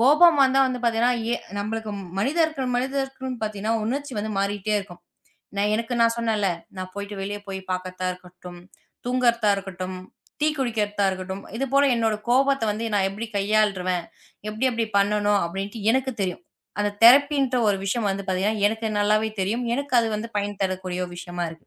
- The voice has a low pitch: No, high, 215 Hz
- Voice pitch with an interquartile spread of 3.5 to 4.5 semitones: Yes, average, 4.0 semitones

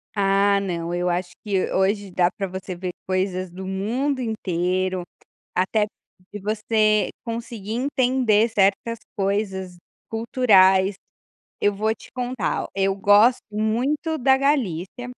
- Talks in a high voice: Yes, high, 205 Hz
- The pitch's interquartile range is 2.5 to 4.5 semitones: Yes, average, 3.5 semitones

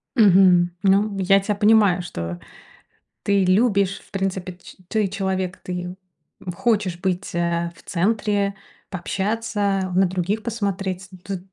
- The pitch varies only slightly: Yes, narrow, 2.1 semitones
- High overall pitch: Yes, high, 195 Hz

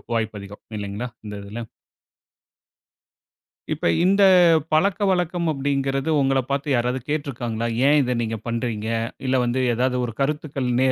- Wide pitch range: No, average, 3.8 semitones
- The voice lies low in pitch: Yes, low, 130 Hz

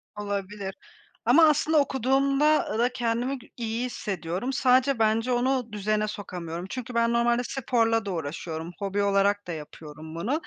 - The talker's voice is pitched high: Yes, high, 225 Hz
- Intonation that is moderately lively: Yes, average, 4.3 semitones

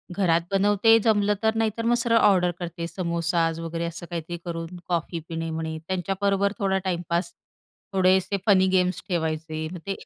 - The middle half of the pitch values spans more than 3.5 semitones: No, average, 2.9 semitones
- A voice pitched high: No, medium, 180 Hz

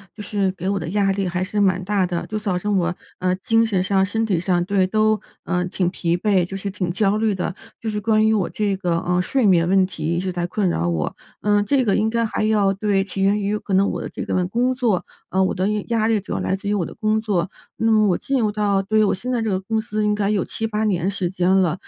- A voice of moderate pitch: No, high, 195 Hz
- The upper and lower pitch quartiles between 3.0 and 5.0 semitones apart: No, narrow, 2.6 semitones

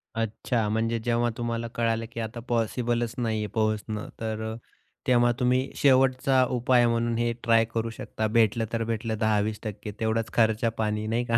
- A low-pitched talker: Yes, low, 115 Hz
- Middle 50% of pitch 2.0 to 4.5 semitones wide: No, narrow, 1.4 semitones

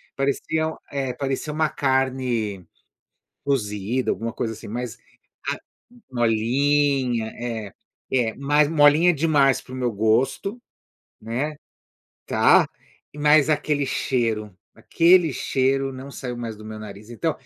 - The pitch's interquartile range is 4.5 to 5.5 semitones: No, average, 4.1 semitones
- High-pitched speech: No, low, 130 Hz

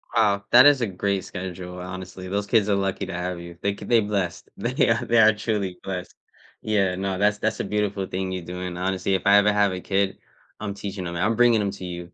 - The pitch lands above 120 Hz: No, low, 100 Hz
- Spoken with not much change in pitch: Yes, narrow, 2.2 semitones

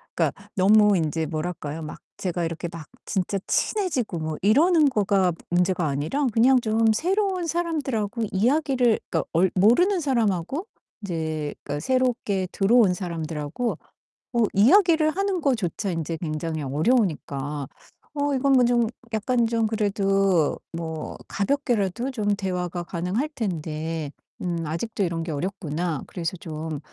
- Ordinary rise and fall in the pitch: No, wide, 7.0 semitones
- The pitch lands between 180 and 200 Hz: Yes, high, 195 Hz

